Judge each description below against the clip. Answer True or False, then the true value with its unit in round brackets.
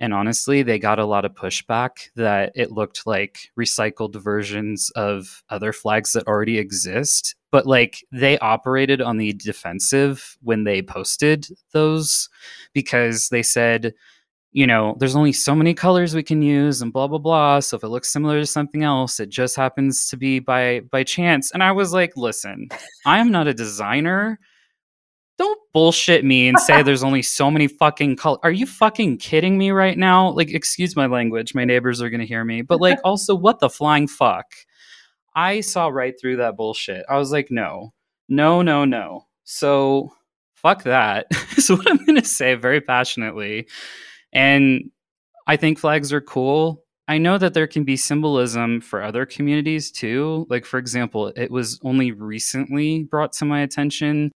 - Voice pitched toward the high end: False (135 Hz)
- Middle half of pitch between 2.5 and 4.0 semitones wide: False (4.7 semitones)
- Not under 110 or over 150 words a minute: False (180 wpm)